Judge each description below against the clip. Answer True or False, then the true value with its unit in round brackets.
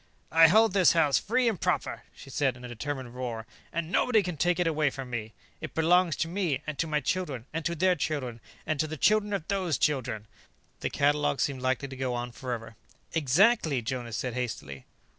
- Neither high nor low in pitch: True (145 Hz)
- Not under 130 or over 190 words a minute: False (205 wpm)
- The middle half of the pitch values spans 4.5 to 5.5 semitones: True (5.2 semitones)